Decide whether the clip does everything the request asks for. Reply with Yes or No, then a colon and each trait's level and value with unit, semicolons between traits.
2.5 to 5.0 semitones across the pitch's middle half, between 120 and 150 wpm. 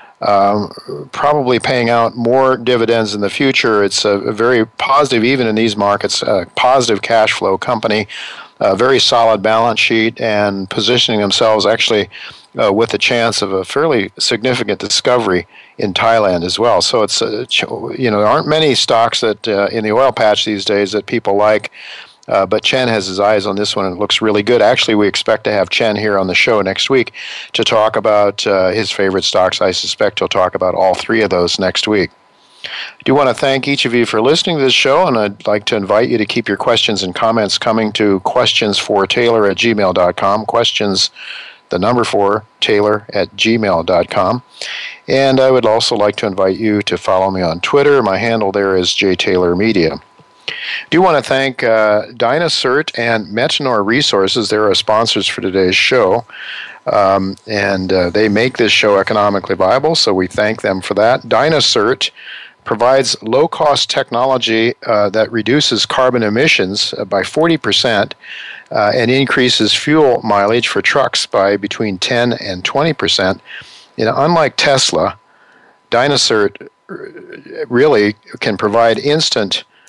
No: average, 2.9 semitones; average, 175 wpm